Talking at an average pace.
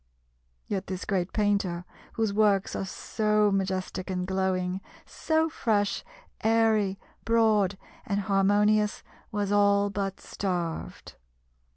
No: slow, 105 wpm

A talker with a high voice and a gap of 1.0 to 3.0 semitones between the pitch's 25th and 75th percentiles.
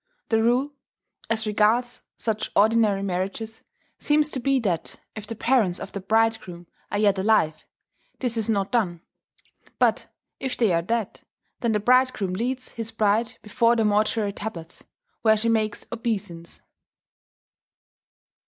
Yes: high, 220 Hz; narrow, 2.6 semitones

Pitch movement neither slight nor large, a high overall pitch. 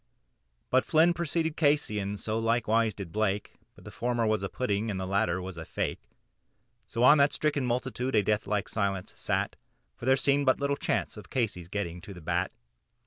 No: average, 4.9 semitones; low, 110 Hz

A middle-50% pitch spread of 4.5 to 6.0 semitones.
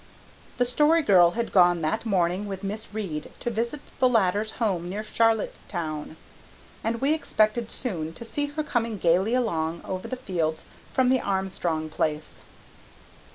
Yes: average, 5.3 semitones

